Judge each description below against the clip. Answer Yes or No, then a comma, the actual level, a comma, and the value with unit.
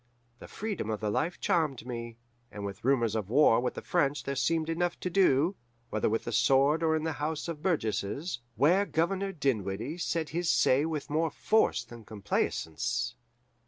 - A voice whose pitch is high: No, medium, 145 Hz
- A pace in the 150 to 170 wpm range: No, average, 180 wpm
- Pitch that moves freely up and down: Yes, wide, 6.1 semitones